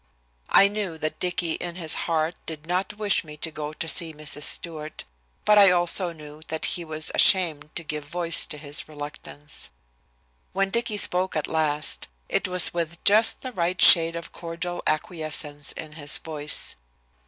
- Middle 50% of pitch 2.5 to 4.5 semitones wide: Yes, average, 2.8 semitones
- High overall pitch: No, medium, 165 Hz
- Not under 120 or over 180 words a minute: Yes, average, 170 wpm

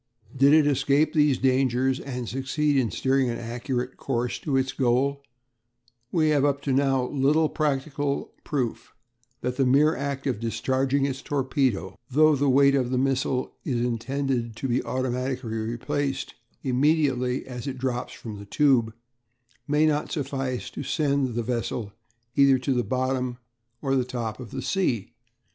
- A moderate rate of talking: Yes, average, 150 wpm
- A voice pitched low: Yes, low, 130 Hz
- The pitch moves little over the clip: Yes, narrow, 2.2 semitones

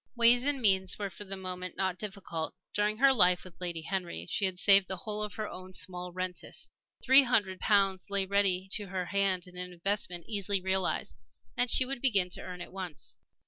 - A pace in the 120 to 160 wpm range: No, fast, 205 wpm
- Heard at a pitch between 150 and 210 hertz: Yes, high, 190 Hz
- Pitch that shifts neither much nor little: No, narrow, 2.3 semitones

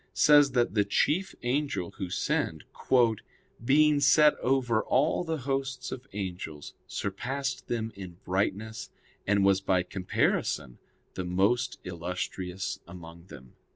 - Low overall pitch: Yes, low, 105 Hz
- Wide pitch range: Yes, wide, 6.7 semitones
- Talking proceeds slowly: Yes, slow, 120 wpm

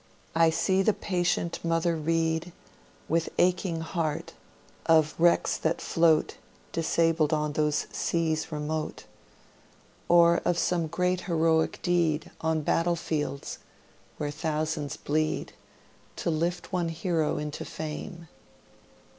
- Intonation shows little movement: Yes, narrow, 1.6 semitones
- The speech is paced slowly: Yes, slow, 115 wpm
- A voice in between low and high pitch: Yes, medium, 165 Hz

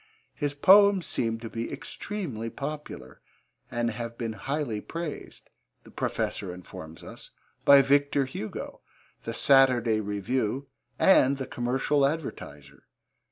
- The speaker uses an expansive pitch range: No, average, 4.1 semitones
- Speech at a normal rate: No, slow, 115 wpm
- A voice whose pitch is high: No, low, 130 Hz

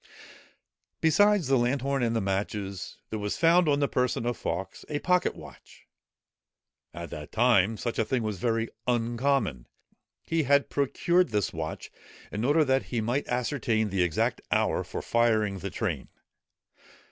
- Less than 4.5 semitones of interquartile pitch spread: No, average, 5.2 semitones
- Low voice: Yes, low, 120 Hz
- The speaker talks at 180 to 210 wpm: No, average, 155 wpm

